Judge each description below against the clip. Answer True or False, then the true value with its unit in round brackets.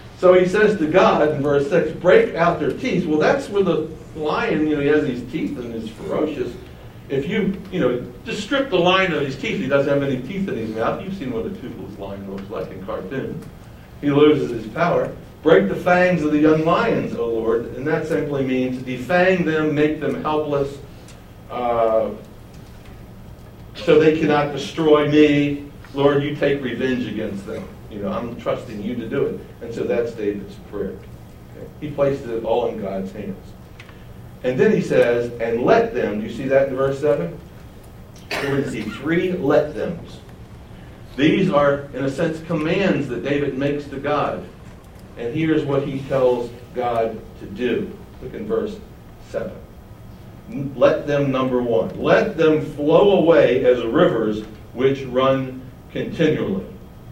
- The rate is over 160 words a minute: True (170 wpm)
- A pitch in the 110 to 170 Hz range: True (140 Hz)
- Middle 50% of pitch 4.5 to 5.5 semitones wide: False (3.9 semitones)